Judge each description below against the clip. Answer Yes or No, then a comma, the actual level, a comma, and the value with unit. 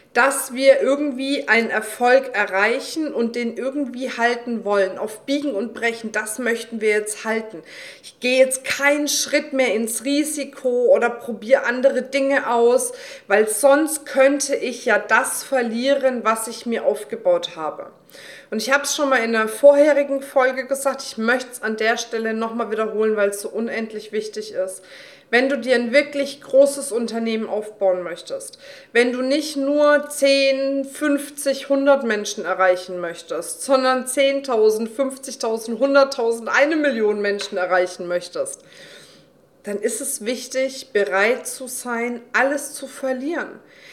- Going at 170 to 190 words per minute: No, average, 150 wpm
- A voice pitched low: No, very high, 250 Hz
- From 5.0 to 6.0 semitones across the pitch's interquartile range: No, average, 4.0 semitones